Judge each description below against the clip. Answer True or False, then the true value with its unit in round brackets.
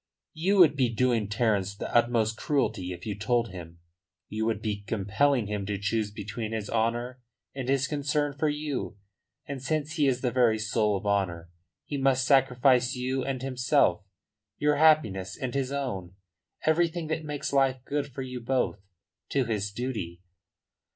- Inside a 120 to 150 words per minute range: False (165 wpm)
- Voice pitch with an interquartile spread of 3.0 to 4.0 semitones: False (4.7 semitones)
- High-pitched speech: False (125 Hz)